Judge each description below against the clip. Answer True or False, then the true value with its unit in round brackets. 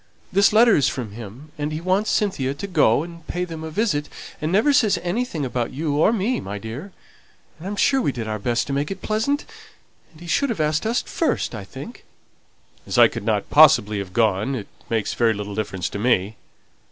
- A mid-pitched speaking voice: True (150 Hz)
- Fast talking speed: True (210 wpm)